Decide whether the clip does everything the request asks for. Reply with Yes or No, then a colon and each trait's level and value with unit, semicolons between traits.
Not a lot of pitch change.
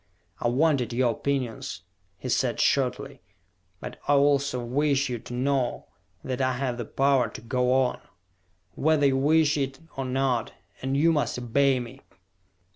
Yes: narrow, 2.1 semitones